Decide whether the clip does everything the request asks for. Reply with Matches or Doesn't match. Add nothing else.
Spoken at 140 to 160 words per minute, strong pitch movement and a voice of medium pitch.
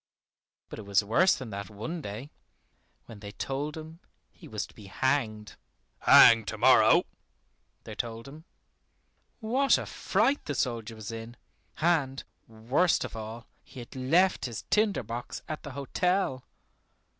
Doesn't match